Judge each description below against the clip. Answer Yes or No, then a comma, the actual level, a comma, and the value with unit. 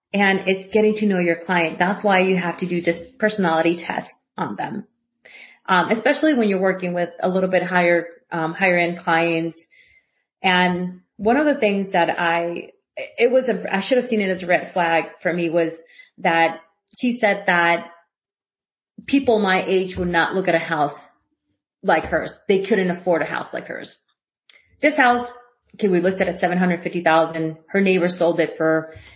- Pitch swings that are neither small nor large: Yes, average, 3.6 semitones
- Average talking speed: Yes, average, 190 wpm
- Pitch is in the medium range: Yes, medium, 180 Hz